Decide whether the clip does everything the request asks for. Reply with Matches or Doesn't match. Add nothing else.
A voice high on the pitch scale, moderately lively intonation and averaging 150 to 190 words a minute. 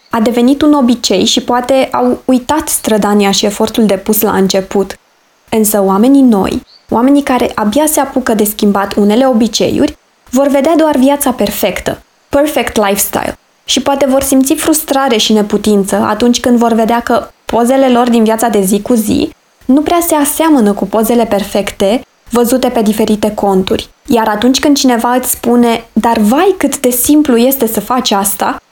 Matches